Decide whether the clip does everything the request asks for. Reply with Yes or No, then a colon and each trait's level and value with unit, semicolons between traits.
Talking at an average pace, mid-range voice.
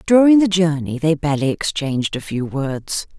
Yes: average, 170 wpm; medium, 155 Hz